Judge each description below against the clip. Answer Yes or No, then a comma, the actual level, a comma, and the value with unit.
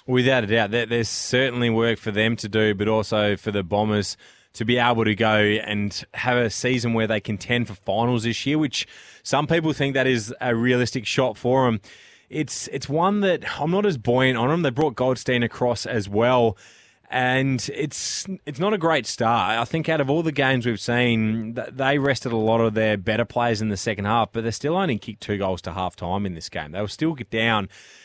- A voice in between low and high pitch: No, low, 120 Hz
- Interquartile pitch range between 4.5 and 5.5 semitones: No, average, 3.3 semitones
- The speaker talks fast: Yes, fast, 220 wpm